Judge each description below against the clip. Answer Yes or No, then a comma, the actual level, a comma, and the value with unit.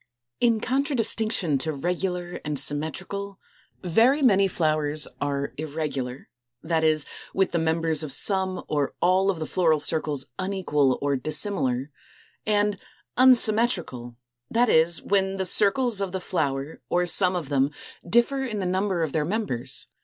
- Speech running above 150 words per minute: No, average, 145 wpm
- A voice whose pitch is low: No, medium, 175 Hz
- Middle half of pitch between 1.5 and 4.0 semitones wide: No, average, 5.0 semitones